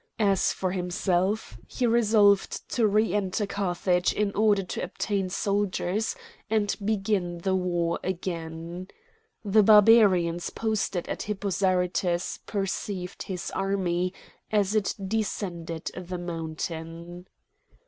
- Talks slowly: Yes, slow, 110 wpm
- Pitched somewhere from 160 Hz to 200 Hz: Yes, high, 190 Hz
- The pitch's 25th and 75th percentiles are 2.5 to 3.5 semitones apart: Yes, average, 2.8 semitones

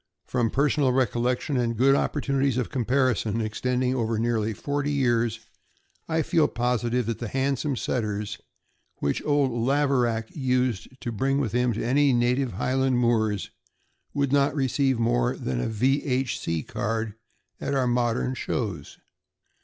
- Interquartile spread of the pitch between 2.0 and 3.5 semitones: Yes, average, 2.9 semitones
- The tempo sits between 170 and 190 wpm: No, average, 145 wpm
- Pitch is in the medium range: No, low, 125 Hz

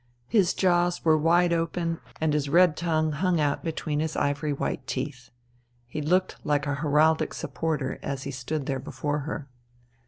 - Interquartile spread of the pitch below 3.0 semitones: Yes, narrow, 2.6 semitones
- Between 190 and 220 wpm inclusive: No, average, 165 wpm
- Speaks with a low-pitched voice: No, medium, 155 Hz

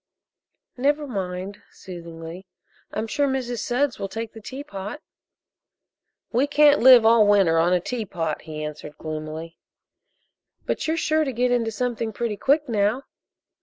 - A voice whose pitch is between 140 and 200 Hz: No, high, 220 Hz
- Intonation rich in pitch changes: Yes, wide, 6.1 semitones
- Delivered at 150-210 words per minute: No, average, 140 wpm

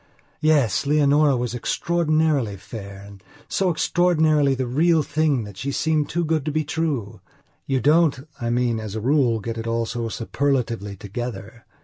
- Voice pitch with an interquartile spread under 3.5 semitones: No, average, 5.3 semitones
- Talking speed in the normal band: Yes, average, 160 wpm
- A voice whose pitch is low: Yes, low, 130 Hz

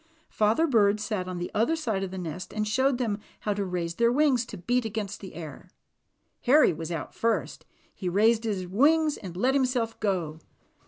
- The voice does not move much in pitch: No, average, 5.0 semitones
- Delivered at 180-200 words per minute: Yes, average, 195 wpm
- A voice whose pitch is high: Yes, high, 210 Hz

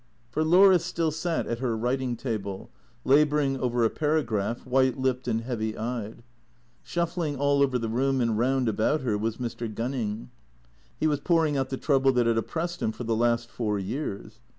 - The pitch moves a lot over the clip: No, average, 3.9 semitones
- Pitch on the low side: Yes, low, 125 Hz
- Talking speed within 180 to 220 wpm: Yes, average, 185 wpm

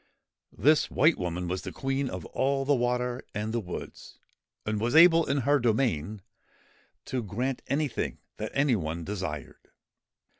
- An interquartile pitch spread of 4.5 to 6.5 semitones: Yes, average, 5.2 semitones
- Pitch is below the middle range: Yes, low, 120 Hz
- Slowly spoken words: No, average, 150 wpm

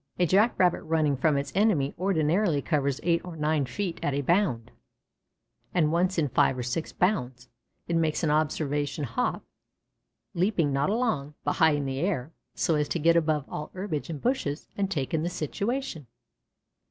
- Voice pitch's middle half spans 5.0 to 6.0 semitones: No, average, 3.9 semitones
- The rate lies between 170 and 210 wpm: Yes, average, 175 wpm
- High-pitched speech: No, medium, 155 Hz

